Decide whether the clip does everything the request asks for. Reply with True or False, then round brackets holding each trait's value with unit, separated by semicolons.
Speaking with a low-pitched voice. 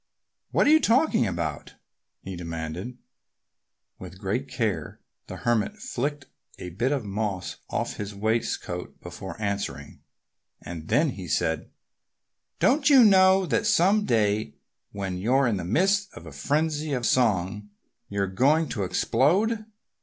True (115 Hz)